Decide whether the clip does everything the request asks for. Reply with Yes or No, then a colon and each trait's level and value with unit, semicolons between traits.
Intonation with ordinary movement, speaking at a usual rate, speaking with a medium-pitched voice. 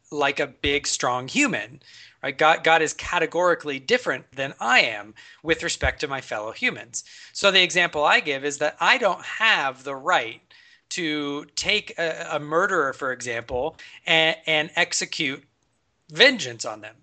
Yes: average, 3.6 semitones; average, 160 wpm; medium, 150 Hz